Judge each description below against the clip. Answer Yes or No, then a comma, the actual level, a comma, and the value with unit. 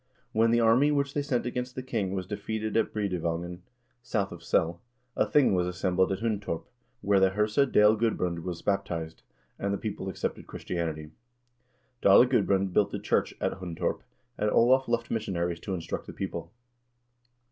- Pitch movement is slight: No, average, 4.2 semitones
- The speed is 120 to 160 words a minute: No, average, 170 wpm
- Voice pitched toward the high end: No, low, 100 Hz